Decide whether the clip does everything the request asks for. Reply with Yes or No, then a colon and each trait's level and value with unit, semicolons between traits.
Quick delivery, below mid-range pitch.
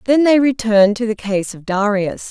No: fast, 210 wpm; high, 220 Hz